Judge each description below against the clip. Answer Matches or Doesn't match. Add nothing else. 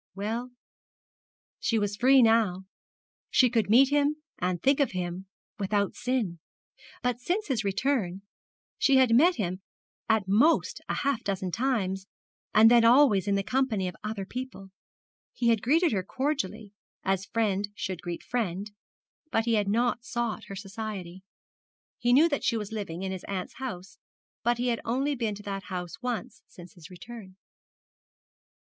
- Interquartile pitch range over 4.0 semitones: Matches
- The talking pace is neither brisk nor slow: Matches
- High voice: Matches